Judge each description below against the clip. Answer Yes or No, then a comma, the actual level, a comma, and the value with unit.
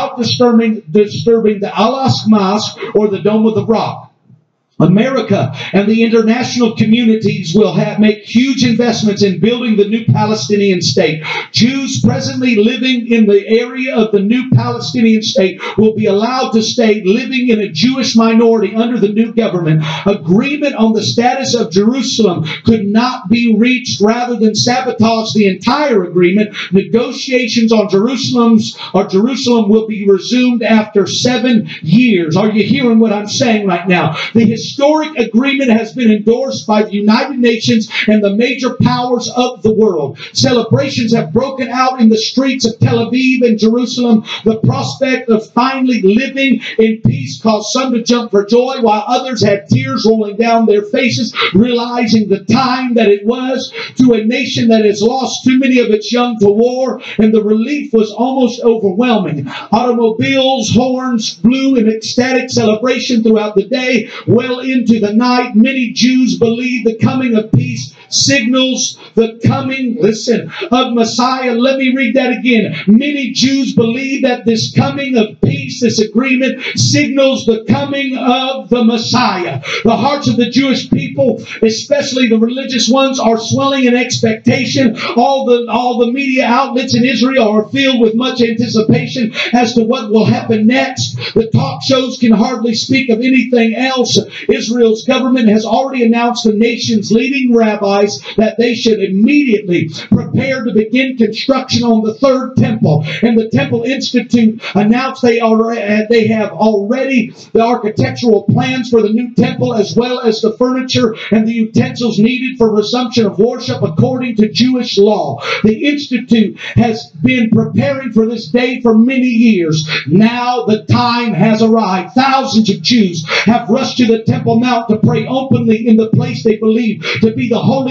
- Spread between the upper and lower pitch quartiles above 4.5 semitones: No, narrow, 2.6 semitones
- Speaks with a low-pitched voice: No, high, 230 Hz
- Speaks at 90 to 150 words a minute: No, average, 160 wpm